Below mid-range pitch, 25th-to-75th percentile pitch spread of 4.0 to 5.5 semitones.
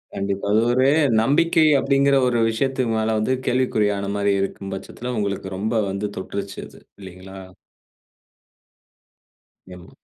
Yes: low, 105 Hz; average, 4.5 semitones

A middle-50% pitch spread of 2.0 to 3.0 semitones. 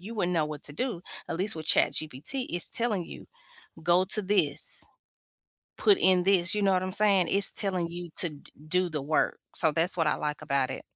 No: average, 3.8 semitones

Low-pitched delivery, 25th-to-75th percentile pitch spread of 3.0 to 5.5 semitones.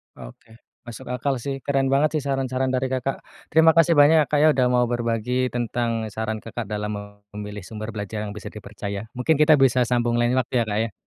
Yes: low, 120 Hz; average, 3.6 semitones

